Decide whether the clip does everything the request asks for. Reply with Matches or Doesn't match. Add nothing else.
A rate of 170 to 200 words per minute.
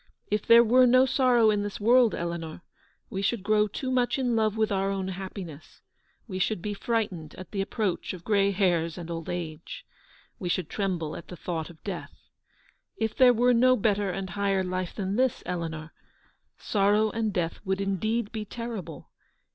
Matches